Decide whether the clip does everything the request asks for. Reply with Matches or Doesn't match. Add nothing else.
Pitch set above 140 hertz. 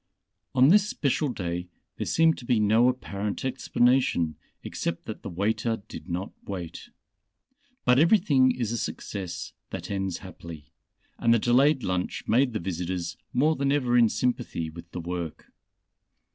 Doesn't match